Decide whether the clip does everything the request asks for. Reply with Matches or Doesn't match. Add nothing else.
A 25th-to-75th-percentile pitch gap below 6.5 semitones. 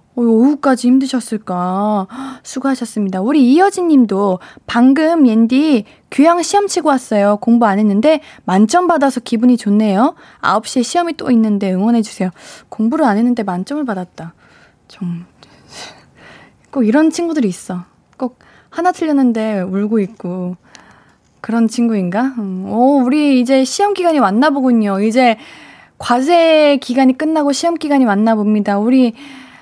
Matches